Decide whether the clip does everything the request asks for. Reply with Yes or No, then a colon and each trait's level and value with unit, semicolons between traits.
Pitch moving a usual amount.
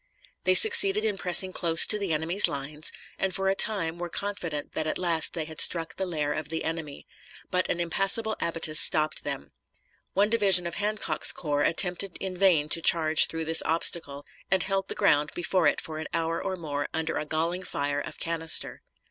Yes: average, 3.4 semitones